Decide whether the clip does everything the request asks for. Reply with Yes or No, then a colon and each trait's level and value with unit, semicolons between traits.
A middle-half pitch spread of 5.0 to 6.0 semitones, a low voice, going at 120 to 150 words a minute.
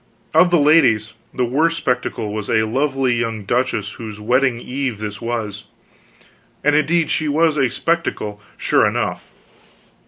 Yes: average, 5.3 semitones; low, 125 Hz; average, 145 wpm